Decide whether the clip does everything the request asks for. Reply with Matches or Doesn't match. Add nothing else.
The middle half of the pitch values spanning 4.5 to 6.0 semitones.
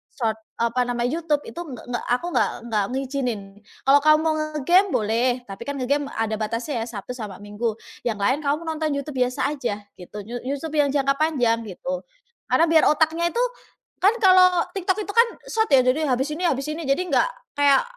Matches